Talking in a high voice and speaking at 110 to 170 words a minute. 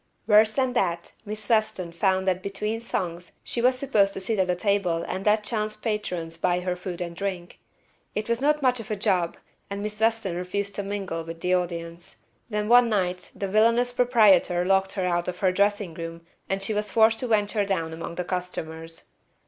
No: high, 195 Hz; average, 200 wpm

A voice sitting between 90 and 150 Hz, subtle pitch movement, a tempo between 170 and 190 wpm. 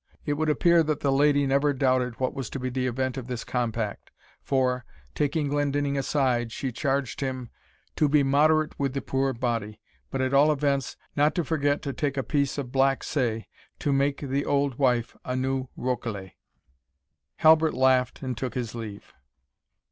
Yes: low, 135 Hz; narrow, 2.2 semitones; average, 180 wpm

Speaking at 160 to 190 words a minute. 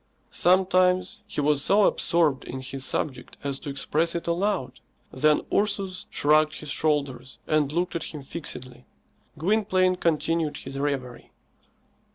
No: slow, 135 wpm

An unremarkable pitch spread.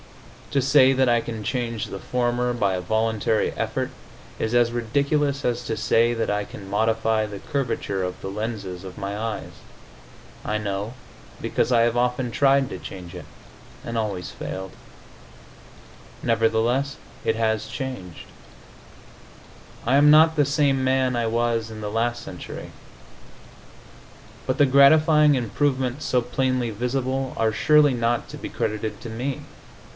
Yes: average, 3.3 semitones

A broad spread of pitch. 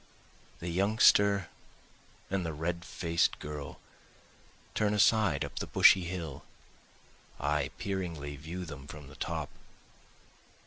No: average, 4.3 semitones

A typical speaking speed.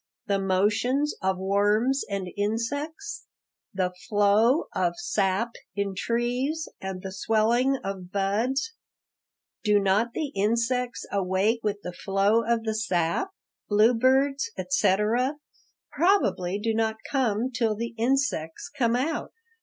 No: slow, 120 wpm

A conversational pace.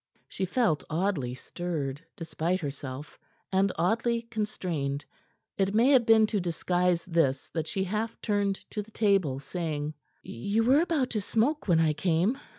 Yes: average, 155 wpm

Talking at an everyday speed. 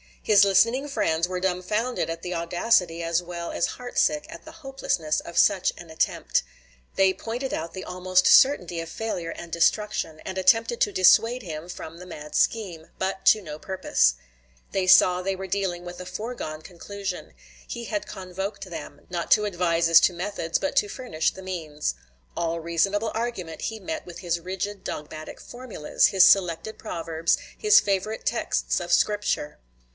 Yes: average, 170 wpm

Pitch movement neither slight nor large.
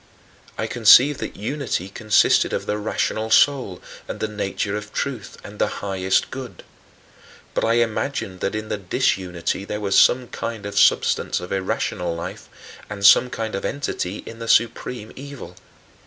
Yes: average, 3.3 semitones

